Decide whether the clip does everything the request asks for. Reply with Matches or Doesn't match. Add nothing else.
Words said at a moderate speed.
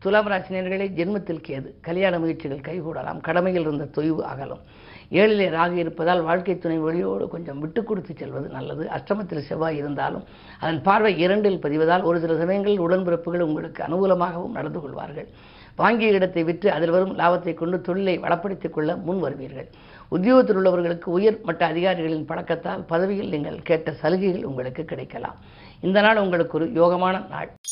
Doesn't match